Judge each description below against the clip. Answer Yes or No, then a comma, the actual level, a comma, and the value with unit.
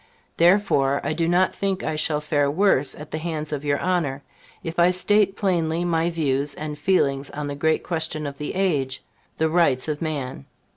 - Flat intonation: No, average, 3.3 semitones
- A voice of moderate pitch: Yes, medium, 155 Hz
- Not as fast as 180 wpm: No, average, 190 wpm